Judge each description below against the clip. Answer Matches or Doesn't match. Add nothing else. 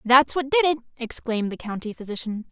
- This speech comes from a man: Doesn't match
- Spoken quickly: Doesn't match